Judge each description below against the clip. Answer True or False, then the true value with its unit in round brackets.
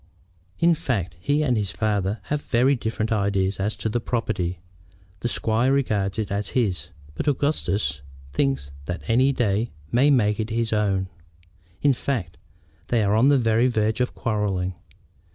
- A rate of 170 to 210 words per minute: False (160 wpm)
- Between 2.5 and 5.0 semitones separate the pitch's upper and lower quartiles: True (4.0 semitones)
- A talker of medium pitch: False (110 Hz)